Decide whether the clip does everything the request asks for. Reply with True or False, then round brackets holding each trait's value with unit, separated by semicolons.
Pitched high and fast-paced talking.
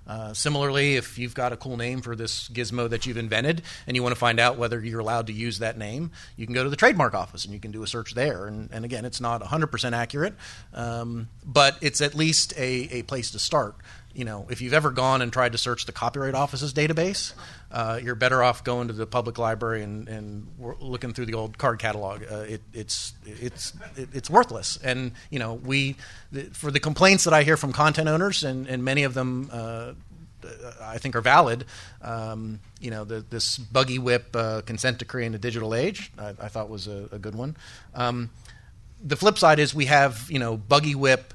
False (120 Hz; 220 wpm)